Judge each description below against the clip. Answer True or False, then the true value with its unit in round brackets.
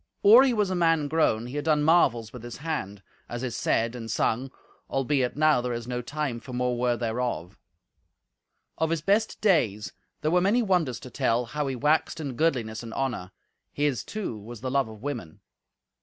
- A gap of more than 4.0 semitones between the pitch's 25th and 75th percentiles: True (5.1 semitones)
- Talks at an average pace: True (195 wpm)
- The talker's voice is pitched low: True (130 Hz)